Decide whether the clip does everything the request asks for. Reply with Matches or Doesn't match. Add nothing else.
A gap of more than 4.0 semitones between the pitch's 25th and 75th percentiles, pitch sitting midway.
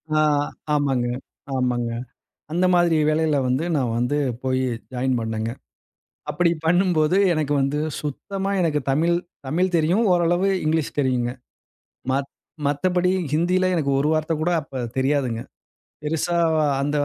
Matches